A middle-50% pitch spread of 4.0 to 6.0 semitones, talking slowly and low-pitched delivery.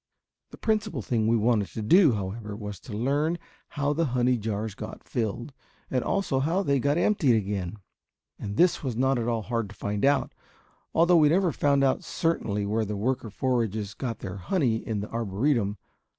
No: wide, 5.4 semitones; average, 185 wpm; low, 120 Hz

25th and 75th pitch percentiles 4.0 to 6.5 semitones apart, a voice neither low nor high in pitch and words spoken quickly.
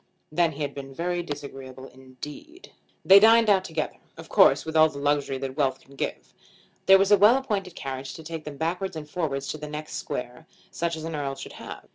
Yes: average, 4.5 semitones; medium, 155 Hz; fast, 215 wpm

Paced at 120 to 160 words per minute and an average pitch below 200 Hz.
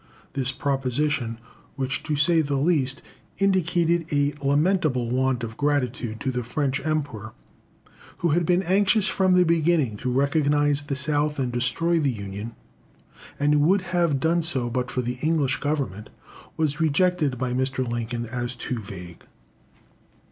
Yes: average, 150 wpm; medium, 140 Hz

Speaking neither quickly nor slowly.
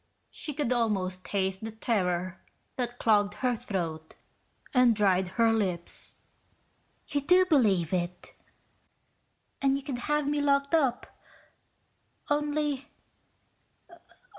No: slow, 110 wpm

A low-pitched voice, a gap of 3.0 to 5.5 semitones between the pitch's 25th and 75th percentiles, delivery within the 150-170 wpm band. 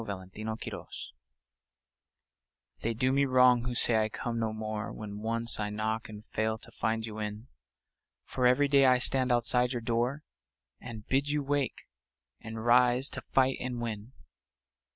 No: low, 115 Hz; narrow, 2.6 semitones; average, 155 wpm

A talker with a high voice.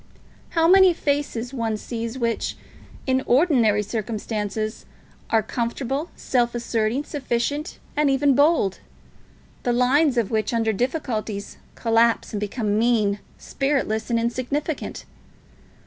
Yes: high, 235 Hz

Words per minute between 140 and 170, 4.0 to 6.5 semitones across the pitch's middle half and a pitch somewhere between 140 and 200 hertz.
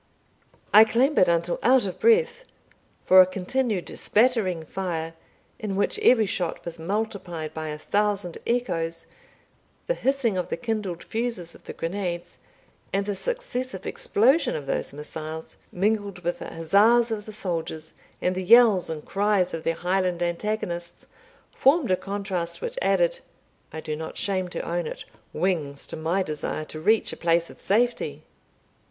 Yes: average, 155 wpm; average, 4.7 semitones; high, 190 Hz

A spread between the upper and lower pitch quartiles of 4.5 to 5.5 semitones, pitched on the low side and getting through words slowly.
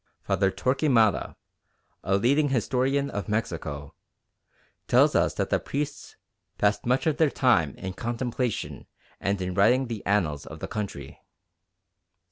Yes: average, 5.2 semitones; low, 110 Hz; slow, 130 wpm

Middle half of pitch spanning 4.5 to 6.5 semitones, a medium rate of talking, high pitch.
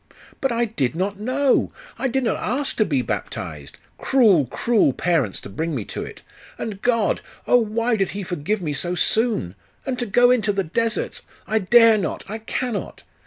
Yes: wide, 5.4 semitones; average, 185 wpm; high, 215 Hz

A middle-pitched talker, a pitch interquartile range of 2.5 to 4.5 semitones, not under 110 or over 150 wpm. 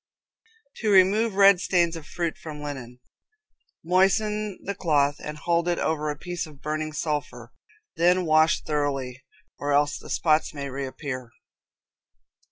Yes: medium, 155 Hz; average, 3.7 semitones; average, 140 wpm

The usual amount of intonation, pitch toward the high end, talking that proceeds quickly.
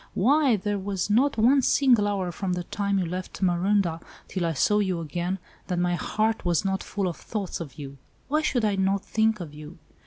Yes: average, 3.3 semitones; high, 195 Hz; fast, 210 wpm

